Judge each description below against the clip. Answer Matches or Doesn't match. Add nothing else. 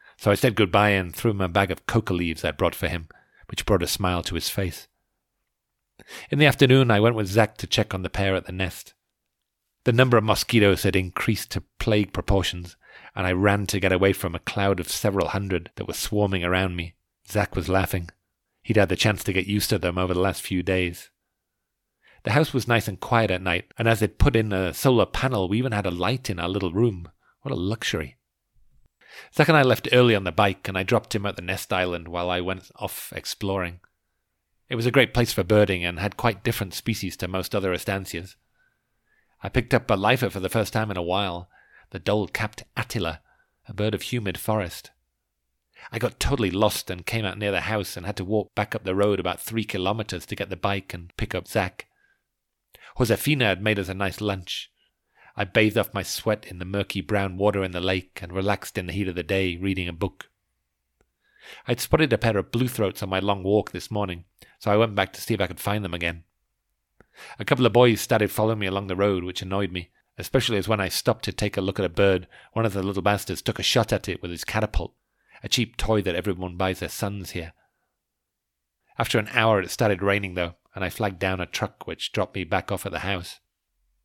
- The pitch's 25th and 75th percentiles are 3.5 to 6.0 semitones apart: Doesn't match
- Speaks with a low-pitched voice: Matches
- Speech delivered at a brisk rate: Matches